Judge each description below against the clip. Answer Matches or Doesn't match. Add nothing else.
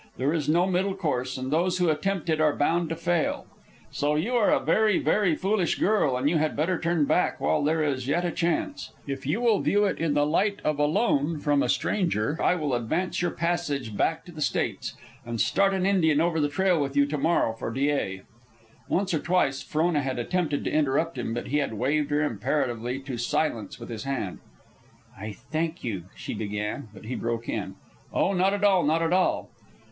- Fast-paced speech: Matches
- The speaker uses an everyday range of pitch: Matches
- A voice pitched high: Doesn't match